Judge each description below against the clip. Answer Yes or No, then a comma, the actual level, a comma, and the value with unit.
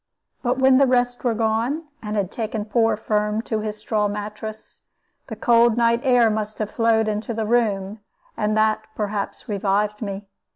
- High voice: Yes, high, 220 Hz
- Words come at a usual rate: Yes, average, 170 wpm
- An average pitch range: No, narrow, 1.8 semitones